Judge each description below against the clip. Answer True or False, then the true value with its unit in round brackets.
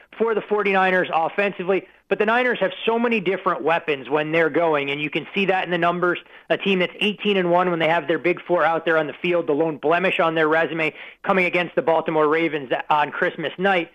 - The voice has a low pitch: False (175 Hz)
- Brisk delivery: True (235 wpm)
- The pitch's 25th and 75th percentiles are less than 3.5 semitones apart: True (3.0 semitones)